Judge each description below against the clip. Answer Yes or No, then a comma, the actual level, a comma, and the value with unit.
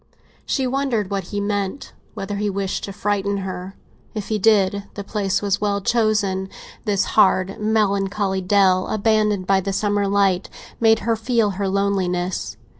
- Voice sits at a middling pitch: No, high, 200 Hz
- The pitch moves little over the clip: Yes, narrow, 1.6 semitones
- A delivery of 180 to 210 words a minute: No, average, 150 wpm